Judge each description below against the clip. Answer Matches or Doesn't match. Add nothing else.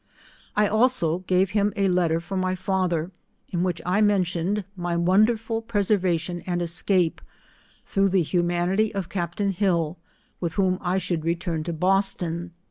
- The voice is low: Doesn't match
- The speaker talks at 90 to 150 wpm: Matches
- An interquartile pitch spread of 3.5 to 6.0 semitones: Doesn't match